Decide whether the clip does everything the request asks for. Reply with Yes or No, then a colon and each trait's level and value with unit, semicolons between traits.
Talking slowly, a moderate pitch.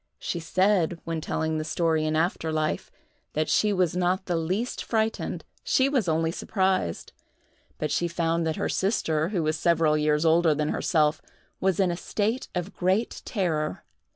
No: average, 165 wpm; medium, 170 Hz